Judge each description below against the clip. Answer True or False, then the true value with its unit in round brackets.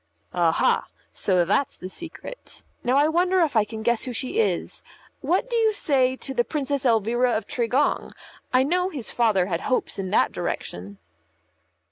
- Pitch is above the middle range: True (255 Hz)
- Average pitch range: False (6.0 semitones)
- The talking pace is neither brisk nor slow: True (170 wpm)